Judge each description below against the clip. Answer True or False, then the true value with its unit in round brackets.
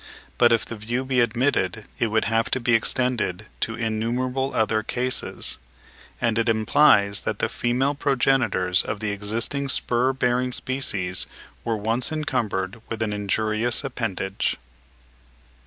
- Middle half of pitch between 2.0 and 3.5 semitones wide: True (2.9 semitones)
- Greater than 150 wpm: False (140 wpm)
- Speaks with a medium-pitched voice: False (115 Hz)